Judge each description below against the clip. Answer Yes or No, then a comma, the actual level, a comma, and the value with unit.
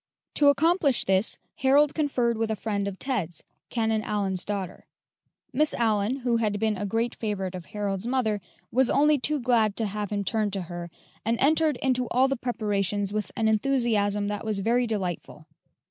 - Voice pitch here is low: No, high, 220 Hz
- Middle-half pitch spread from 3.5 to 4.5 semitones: Yes, average, 3.8 semitones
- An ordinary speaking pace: Yes, average, 175 wpm